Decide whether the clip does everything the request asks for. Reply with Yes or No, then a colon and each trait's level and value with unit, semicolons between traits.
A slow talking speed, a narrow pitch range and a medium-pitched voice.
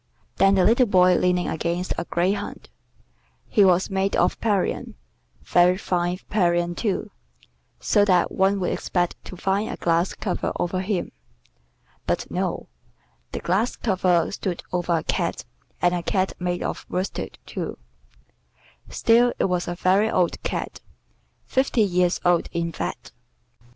No: average, 145 wpm; narrow, 2.0 semitones; medium, 180 Hz